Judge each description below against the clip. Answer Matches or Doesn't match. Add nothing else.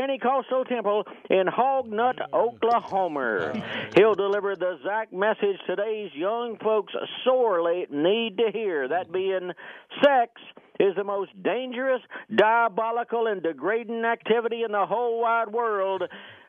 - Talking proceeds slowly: Matches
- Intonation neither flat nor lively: Matches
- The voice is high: Matches